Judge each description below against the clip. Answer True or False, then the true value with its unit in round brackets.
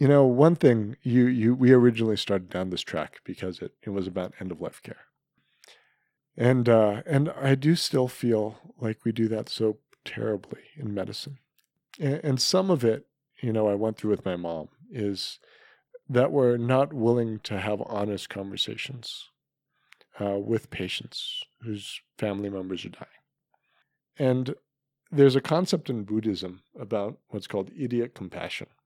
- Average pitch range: True (4.9 semitones)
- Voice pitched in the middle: False (115 Hz)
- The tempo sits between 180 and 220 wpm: False (160 wpm)